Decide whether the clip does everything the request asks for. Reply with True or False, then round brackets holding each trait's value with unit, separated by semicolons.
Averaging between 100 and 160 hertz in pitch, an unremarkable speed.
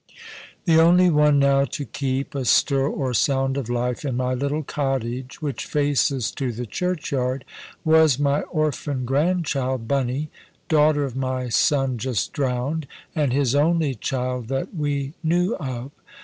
True (140 Hz; 150 wpm)